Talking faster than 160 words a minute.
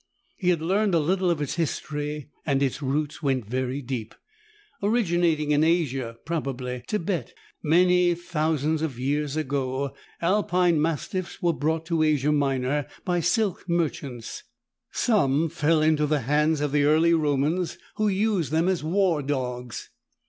No: average, 145 wpm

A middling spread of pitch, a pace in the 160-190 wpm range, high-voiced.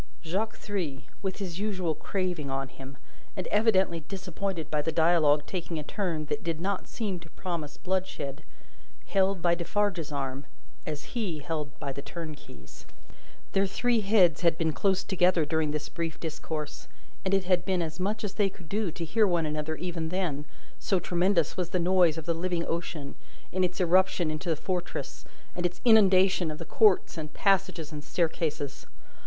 No: average, 3.5 semitones; average, 175 wpm; medium, 175 Hz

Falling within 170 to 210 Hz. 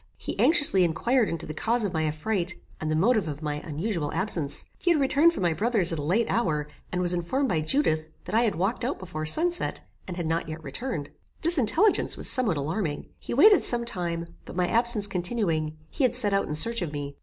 Yes: medium, 185 Hz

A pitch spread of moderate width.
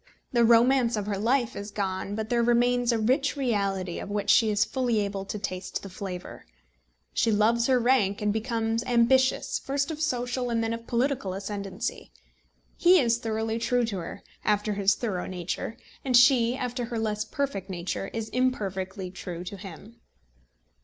Yes: average, 3.6 semitones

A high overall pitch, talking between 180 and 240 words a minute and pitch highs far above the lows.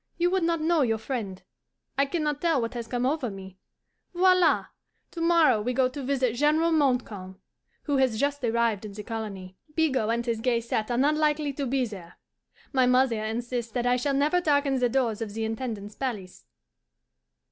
No: very high, 250 Hz; average, 190 wpm; average, 4.5 semitones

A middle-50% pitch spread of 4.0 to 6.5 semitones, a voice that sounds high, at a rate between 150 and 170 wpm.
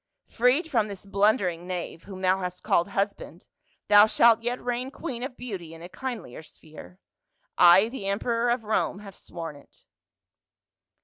Yes: average, 5.0 semitones; high, 200 Hz; average, 160 wpm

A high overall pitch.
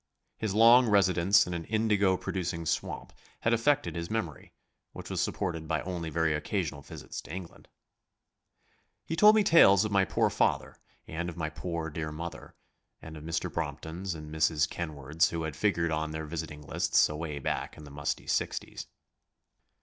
No: very low, 85 Hz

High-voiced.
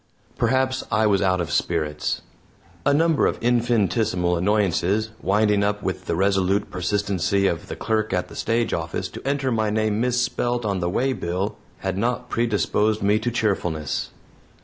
No: low, 105 Hz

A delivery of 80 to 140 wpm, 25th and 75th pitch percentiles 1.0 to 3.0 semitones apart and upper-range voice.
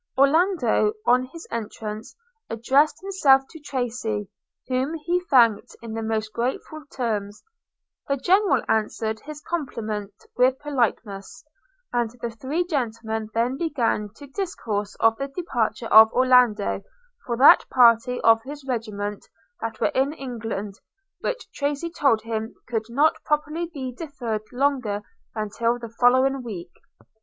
No: slow, 135 wpm; average, 4.3 semitones; high, 245 Hz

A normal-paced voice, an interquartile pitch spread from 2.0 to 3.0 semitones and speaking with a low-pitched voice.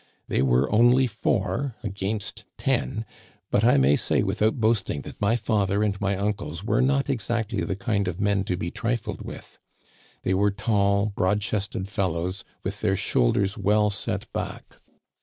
Yes: average, 165 wpm; narrow, 2.5 semitones; low, 100 Hz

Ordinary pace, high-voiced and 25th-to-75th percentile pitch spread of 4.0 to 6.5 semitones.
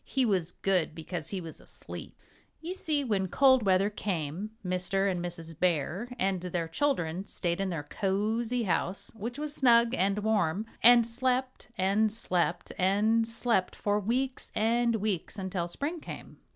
Yes: average, 155 wpm; high, 200 Hz; average, 4.6 semitones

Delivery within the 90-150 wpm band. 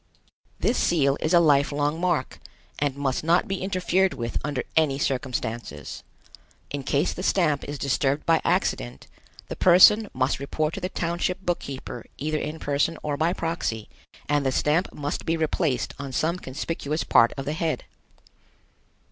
No: average, 165 wpm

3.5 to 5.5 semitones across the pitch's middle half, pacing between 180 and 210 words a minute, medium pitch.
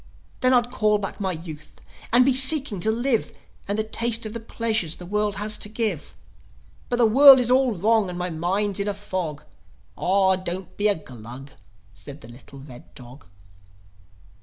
No: average, 5.0 semitones; average, 185 wpm; high, 205 Hz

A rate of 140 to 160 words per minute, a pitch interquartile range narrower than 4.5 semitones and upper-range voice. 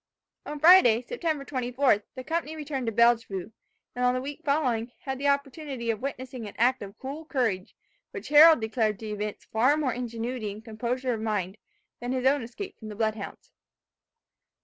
No: average, 180 wpm; average, 4.1 semitones; very high, 250 Hz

